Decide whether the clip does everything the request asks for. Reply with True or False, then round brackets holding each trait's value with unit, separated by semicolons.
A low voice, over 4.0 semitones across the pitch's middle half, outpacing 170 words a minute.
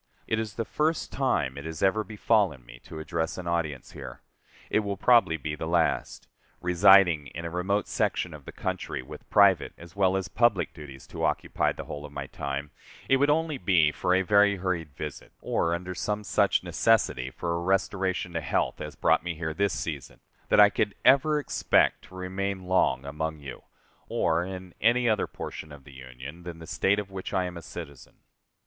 True (90 Hz; 4.5 semitones; 200 wpm)